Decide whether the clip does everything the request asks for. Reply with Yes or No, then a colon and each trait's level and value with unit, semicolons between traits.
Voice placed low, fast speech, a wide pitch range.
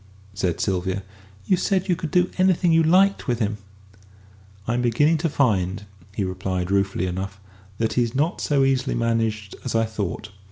No: low, 115 Hz; average, 165 wpm; wide, 7.9 semitones